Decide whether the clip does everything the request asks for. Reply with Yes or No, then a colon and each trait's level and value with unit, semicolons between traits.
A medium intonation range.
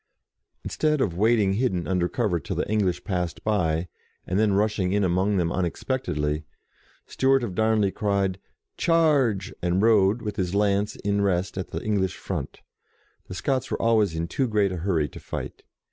Yes: average, 3.3 semitones